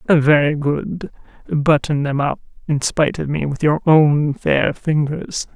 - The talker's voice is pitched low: No, medium, 150 Hz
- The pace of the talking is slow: No, average, 150 wpm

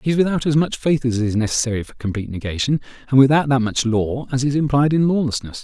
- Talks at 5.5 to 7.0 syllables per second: Yes, 6.4 syllables/s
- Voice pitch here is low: Yes, low, 130 Hz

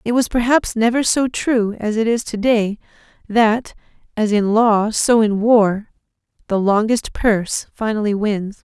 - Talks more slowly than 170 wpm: Yes, average, 150 wpm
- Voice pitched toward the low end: No, high, 220 Hz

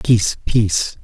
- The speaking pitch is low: Yes, low, 105 Hz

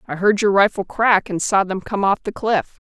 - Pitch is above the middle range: Yes, high, 200 Hz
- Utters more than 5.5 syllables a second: No, 5.1 syllables/s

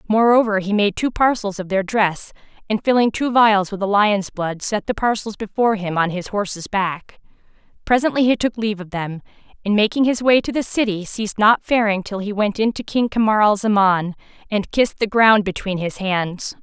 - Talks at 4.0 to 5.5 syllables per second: Yes, 5.2 syllables/s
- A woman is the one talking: Yes, female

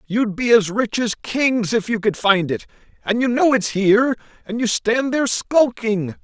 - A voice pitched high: Yes, high, 225 Hz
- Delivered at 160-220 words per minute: Yes, average, 200 wpm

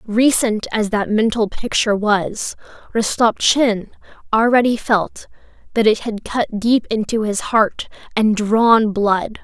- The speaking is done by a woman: Yes, female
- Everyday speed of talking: No, slow, 125 wpm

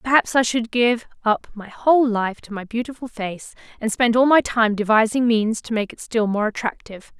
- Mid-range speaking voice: No, high, 225 Hz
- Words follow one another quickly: Yes, fast, 210 wpm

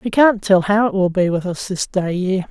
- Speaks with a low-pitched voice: No, high, 195 Hz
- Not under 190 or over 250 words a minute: No, fast, 290 wpm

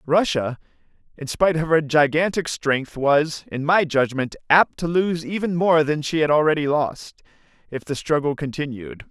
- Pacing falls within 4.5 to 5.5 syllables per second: Yes, 4.6 syllables/s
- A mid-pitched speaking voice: Yes, medium, 155 Hz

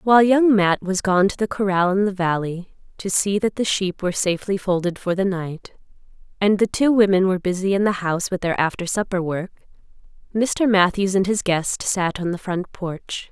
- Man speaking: No, female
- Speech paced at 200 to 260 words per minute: Yes, fast, 205 wpm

